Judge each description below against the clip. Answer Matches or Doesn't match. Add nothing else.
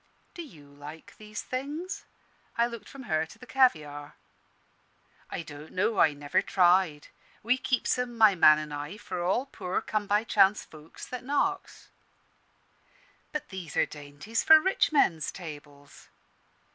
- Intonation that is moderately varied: Doesn't match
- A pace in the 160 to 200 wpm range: Doesn't match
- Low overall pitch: Doesn't match